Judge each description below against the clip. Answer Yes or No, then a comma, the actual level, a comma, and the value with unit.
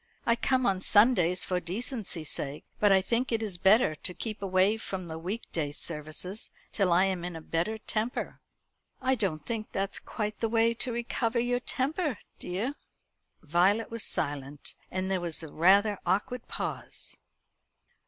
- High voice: Yes, high, 195 Hz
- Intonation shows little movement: No, average, 4.7 semitones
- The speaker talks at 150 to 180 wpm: Yes, average, 165 wpm